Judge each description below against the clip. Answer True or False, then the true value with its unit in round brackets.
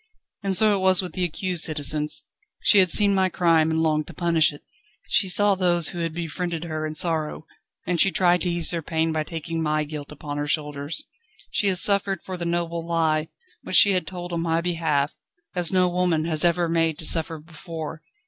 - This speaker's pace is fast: True (215 wpm)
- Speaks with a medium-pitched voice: True (165 Hz)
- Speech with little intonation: True (2.3 semitones)